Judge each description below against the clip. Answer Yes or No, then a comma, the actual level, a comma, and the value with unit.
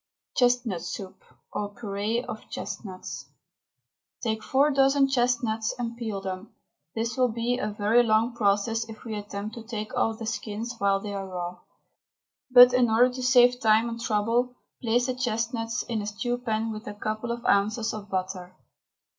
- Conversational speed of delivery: Yes, average, 170 wpm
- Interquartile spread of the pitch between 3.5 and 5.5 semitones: No, average, 2.8 semitones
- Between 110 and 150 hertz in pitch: No, high, 225 Hz